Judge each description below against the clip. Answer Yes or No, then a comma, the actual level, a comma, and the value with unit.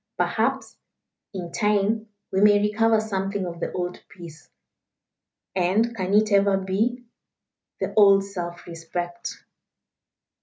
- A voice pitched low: No, high, 195 Hz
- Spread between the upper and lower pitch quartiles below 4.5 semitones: Yes, average, 2.9 semitones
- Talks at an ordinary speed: No, slow, 115 wpm